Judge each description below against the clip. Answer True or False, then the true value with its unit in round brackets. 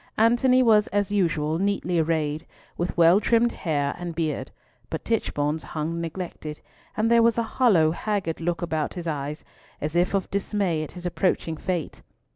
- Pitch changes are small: False (4.4 semitones)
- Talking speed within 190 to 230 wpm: False (165 wpm)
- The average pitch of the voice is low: False (175 Hz)